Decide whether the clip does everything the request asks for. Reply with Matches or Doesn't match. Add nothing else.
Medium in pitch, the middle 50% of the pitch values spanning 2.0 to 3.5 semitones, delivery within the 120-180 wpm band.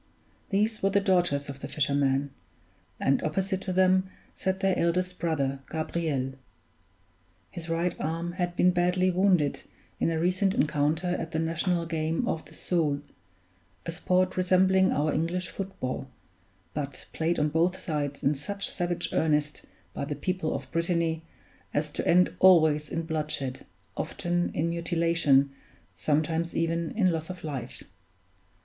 Matches